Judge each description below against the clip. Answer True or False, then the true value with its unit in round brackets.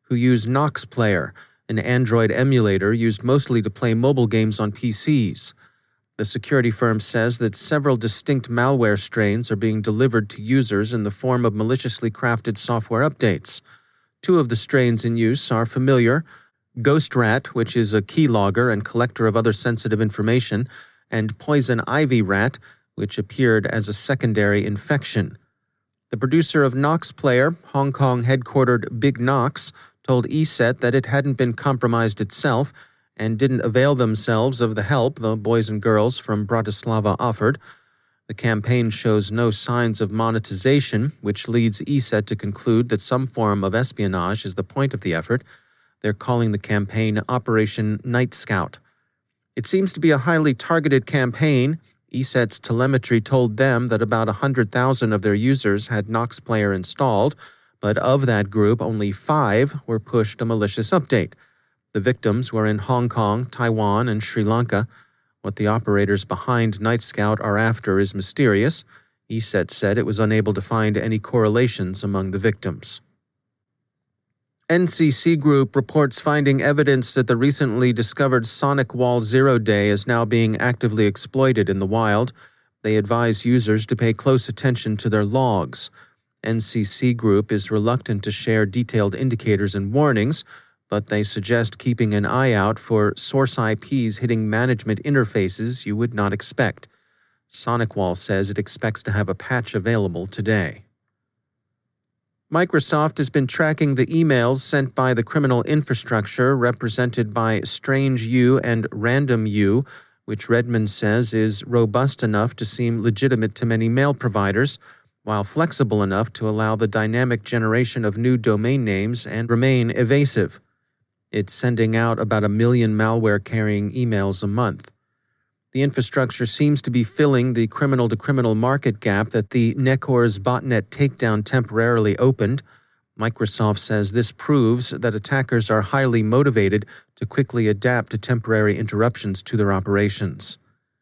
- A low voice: True (115 Hz)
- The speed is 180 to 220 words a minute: False (150 wpm)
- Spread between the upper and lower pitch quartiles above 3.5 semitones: False (3.1 semitones)